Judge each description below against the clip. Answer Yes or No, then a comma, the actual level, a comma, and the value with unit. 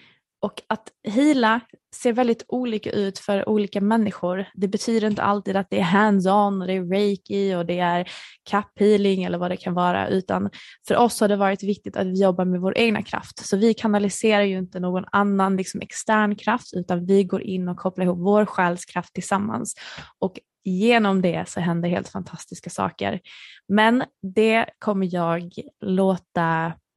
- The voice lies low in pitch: No, high, 195 Hz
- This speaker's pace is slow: No, average, 165 wpm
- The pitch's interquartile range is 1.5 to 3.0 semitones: Yes, narrow, 2.4 semitones